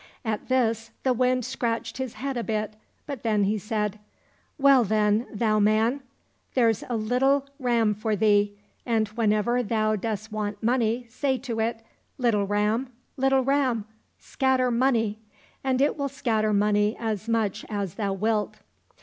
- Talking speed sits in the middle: Yes, average, 160 wpm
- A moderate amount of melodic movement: Yes, average, 3.0 semitones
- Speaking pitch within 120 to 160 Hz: No, high, 225 Hz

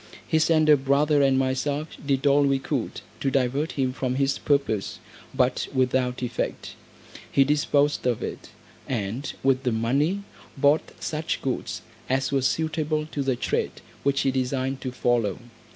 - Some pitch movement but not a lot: No, narrow, 2.1 semitones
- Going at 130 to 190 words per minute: Yes, average, 150 wpm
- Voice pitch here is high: No, low, 135 Hz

